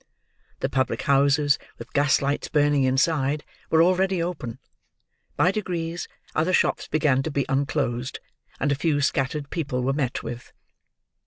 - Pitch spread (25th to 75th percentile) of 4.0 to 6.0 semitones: No, average, 3.2 semitones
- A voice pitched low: No, medium, 145 Hz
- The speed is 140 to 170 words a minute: Yes, average, 145 wpm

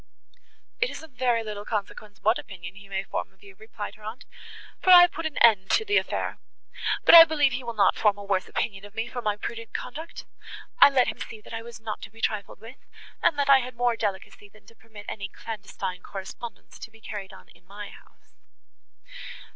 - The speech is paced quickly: Yes, fast, 220 wpm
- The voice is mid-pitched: No, high, 220 Hz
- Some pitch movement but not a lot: Yes, average, 3.4 semitones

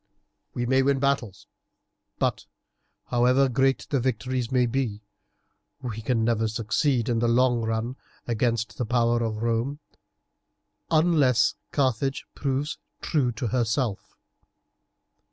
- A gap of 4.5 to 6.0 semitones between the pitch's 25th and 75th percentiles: No, average, 2.7 semitones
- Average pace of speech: No, slow, 115 wpm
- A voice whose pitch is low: Yes, low, 120 Hz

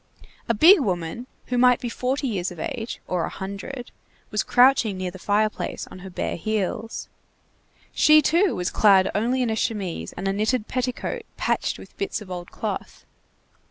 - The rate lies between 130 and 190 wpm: Yes, average, 175 wpm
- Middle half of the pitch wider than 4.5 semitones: Yes, average, 4.9 semitones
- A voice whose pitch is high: Yes, high, 215 Hz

